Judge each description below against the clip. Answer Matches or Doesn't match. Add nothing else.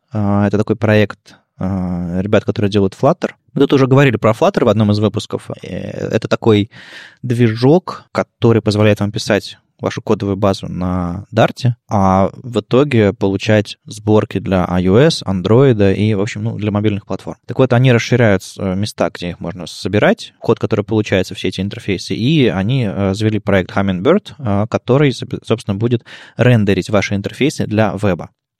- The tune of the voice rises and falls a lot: Doesn't match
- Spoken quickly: Doesn't match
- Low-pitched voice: Matches